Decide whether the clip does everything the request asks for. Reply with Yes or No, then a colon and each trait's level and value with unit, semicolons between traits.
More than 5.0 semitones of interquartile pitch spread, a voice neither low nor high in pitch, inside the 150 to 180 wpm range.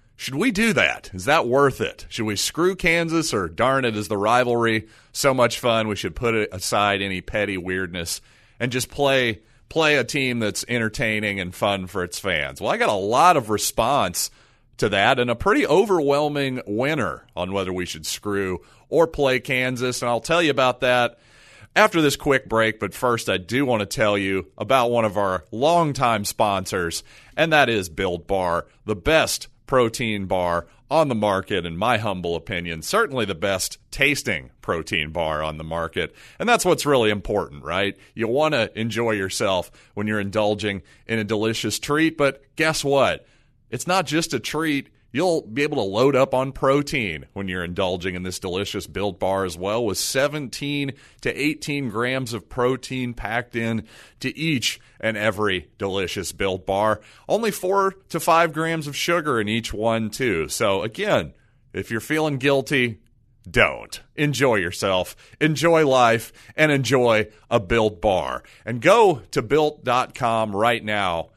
No: wide, 5.4 semitones; low, 115 Hz; average, 170 wpm